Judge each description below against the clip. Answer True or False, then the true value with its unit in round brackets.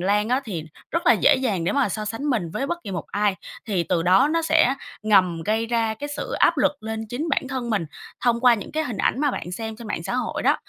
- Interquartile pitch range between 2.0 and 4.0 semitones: False (4.9 semitones)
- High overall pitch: True (225 Hz)